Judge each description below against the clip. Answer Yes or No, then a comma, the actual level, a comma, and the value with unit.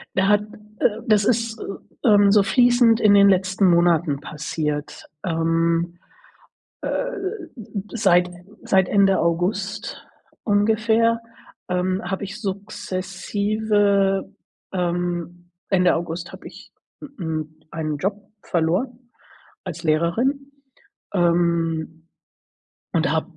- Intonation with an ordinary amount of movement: Yes, average, 3.8 semitones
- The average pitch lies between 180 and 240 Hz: Yes, high, 190 Hz